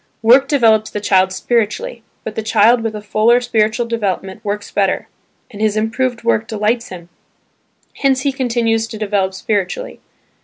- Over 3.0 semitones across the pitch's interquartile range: No, narrow, 2.4 semitones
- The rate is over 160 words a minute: No, average, 155 wpm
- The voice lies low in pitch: No, high, 220 Hz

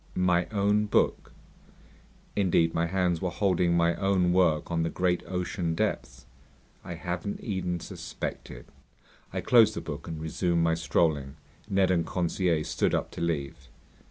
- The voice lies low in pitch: Yes, very low, 85 Hz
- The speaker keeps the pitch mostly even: Yes, narrow, 2.2 semitones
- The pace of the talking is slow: No, average, 150 wpm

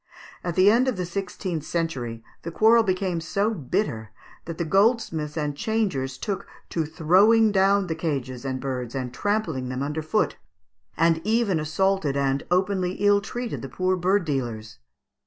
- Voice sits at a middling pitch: Yes, medium, 170 Hz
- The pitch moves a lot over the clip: Yes, wide, 6.1 semitones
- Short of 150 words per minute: No, average, 160 wpm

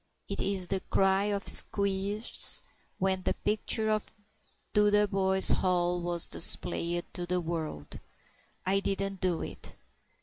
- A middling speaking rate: No, slow, 125 wpm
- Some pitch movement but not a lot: No, narrow, 2.1 semitones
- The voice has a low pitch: No, high, 190 Hz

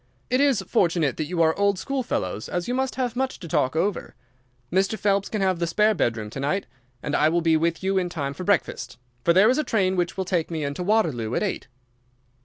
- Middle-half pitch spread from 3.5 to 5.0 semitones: Yes, average, 4.3 semitones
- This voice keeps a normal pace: No, fast, 230 wpm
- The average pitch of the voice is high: No, medium, 180 Hz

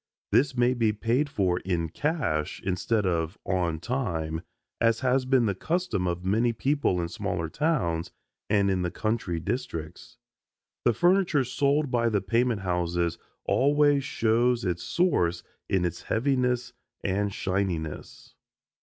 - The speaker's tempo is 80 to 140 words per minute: Yes, slow, 135 wpm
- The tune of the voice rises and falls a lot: Yes, wide, 6.4 semitones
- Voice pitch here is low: Yes, low, 110 Hz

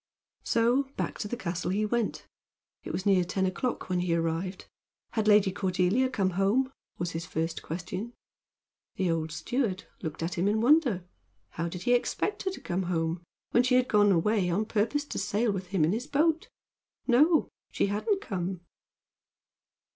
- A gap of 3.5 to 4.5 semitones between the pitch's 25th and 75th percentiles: No, average, 5.3 semitones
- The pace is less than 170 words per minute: No, average, 175 wpm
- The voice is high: Yes, high, 195 Hz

